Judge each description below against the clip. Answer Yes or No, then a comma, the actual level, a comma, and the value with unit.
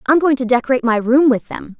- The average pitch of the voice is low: No, very high, 255 Hz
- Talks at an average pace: No, fast, 270 wpm